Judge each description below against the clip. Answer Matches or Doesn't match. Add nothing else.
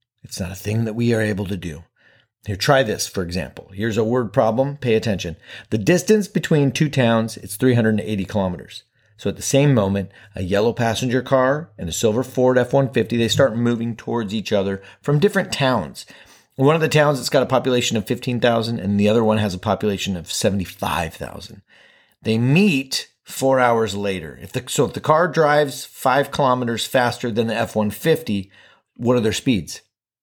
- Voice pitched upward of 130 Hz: Doesn't match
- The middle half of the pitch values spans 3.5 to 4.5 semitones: Matches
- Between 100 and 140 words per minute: Doesn't match